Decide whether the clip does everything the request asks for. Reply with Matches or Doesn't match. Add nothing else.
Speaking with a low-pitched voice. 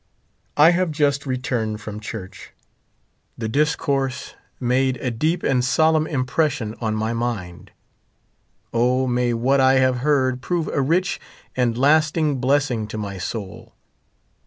Matches